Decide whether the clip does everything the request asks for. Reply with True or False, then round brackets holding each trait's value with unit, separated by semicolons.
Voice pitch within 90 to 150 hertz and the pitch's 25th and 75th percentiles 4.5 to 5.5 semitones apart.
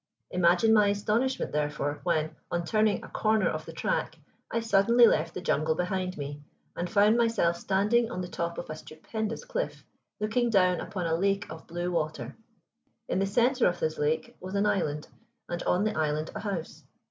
False (185 Hz; 4.9 semitones)